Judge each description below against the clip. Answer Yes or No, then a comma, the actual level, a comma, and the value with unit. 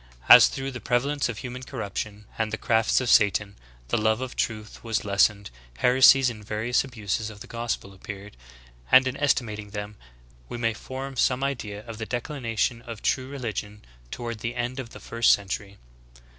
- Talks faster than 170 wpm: Yes, average, 180 wpm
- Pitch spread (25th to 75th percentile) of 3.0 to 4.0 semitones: Yes, average, 3.3 semitones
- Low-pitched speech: Yes, low, 115 Hz